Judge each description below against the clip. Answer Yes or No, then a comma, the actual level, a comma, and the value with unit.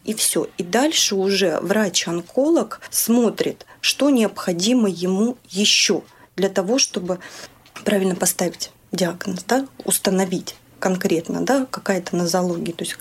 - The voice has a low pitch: No, high, 195 Hz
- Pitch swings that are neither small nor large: Yes, average, 3.4 semitones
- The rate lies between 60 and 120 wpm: Yes, average, 115 wpm